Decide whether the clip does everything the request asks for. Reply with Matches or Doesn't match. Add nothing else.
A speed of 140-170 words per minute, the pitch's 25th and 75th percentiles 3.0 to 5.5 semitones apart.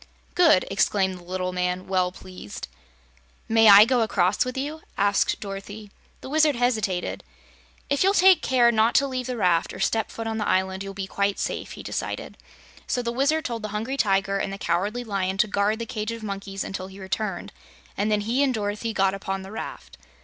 Doesn't match